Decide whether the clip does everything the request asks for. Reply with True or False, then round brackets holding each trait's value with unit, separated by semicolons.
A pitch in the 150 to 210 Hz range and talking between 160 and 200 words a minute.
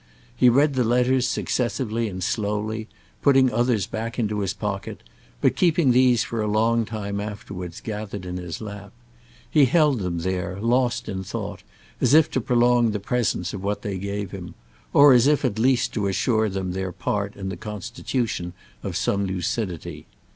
False (110 Hz; 175 wpm)